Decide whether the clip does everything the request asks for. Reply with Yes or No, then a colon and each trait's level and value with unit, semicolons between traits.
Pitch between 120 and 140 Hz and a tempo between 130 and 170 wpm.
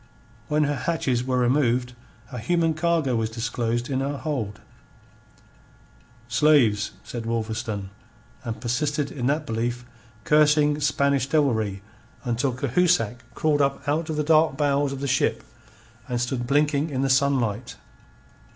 Yes: low, 135 Hz; slow, 135 wpm